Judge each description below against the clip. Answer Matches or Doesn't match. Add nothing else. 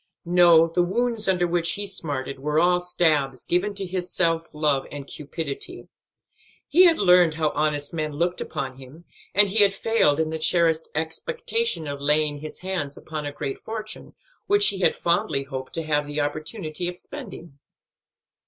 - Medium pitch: Matches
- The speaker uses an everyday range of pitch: Matches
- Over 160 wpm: Matches